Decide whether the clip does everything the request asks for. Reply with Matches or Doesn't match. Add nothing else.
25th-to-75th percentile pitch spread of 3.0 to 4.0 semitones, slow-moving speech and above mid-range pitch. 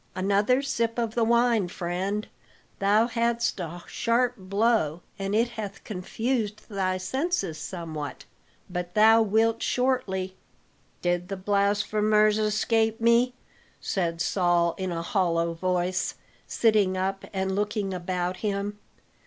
Matches